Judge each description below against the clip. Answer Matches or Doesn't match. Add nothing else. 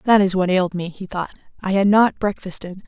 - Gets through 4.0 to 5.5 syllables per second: Doesn't match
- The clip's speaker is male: Doesn't match